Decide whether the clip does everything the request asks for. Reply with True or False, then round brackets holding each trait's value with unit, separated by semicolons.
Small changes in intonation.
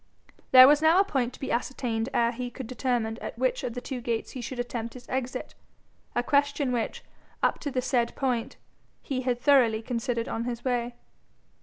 True (2.0 semitones)